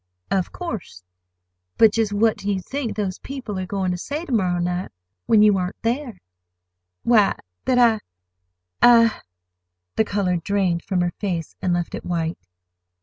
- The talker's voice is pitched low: No, high, 195 Hz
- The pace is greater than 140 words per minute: Yes, average, 150 wpm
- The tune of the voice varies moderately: Yes, average, 4.2 semitones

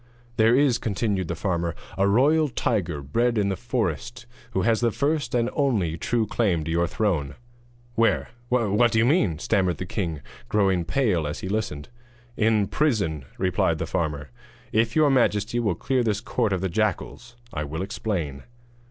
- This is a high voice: No, low, 105 Hz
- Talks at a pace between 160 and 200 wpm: Yes, average, 170 wpm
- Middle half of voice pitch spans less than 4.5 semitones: No, wide, 5.6 semitones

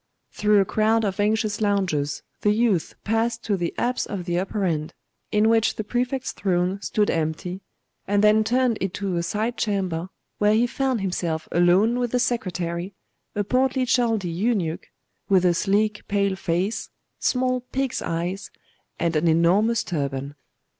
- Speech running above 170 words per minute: No, average, 155 wpm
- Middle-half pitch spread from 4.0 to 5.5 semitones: Yes, average, 4.3 semitones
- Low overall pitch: No, high, 205 Hz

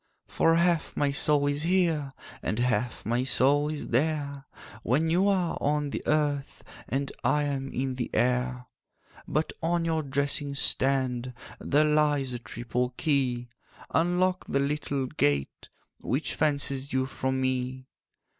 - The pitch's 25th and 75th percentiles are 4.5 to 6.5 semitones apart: No, average, 2.9 semitones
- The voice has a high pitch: No, medium, 140 Hz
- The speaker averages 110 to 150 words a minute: Yes, average, 140 wpm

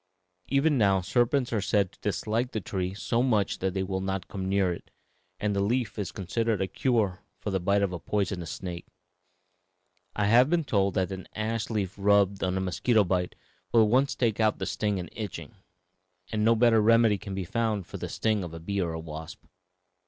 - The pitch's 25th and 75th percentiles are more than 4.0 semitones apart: No, average, 3.1 semitones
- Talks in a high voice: No, low, 100 Hz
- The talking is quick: Yes, fast, 210 wpm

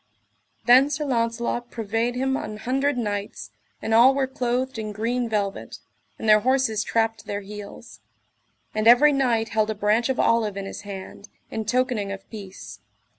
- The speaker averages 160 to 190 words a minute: Yes, average, 170 wpm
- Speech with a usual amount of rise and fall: Yes, average, 3.1 semitones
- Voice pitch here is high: Yes, high, 225 Hz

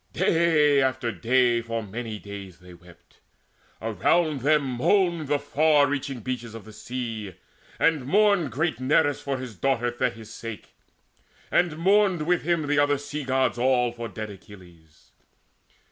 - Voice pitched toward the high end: No, low, 130 Hz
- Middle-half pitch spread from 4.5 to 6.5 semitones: Yes, average, 4.8 semitones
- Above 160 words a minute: No, average, 145 wpm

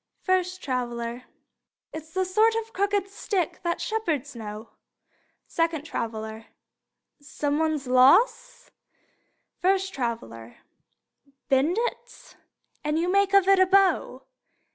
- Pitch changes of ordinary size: No, wide, 7.5 semitones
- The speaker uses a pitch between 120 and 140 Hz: No, very high, 330 Hz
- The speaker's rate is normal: No, slow, 110 wpm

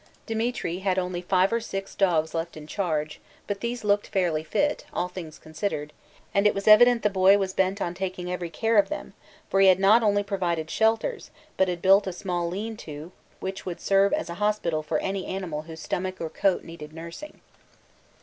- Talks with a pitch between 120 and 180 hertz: No, high, 190 Hz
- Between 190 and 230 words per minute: Yes, average, 200 wpm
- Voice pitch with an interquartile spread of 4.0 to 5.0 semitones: No, average, 3.1 semitones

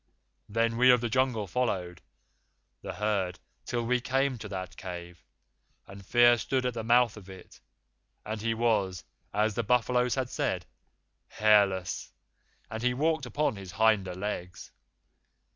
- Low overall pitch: Yes, low, 110 Hz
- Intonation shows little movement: No, average, 4.2 semitones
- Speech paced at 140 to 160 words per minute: Yes, average, 145 wpm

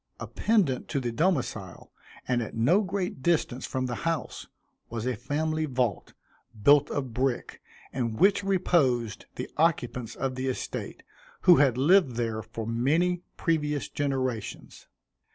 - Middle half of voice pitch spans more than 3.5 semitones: Yes, average, 5.1 semitones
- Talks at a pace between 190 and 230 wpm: No, slow, 135 wpm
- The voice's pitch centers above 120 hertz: Yes, low, 135 Hz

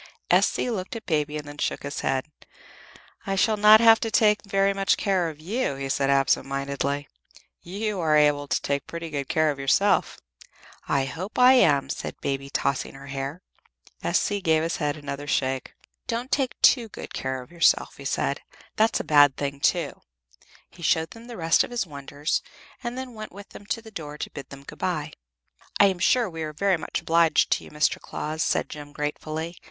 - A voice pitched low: No, medium, 160 Hz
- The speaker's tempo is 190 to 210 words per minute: Yes, average, 200 wpm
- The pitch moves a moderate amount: No, wide, 6.1 semitones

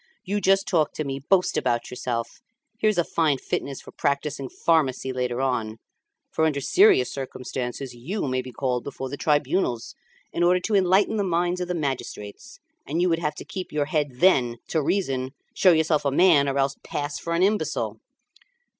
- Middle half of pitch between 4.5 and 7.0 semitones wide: Yes, average, 5.3 semitones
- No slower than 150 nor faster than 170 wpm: No, average, 185 wpm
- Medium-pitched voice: Yes, medium, 145 Hz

